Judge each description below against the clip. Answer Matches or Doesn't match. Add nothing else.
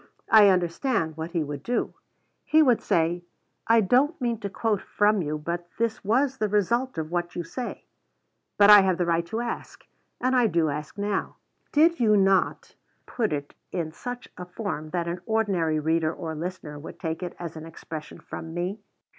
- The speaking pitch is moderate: Matches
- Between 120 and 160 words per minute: Doesn't match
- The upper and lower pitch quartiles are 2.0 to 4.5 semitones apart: Doesn't match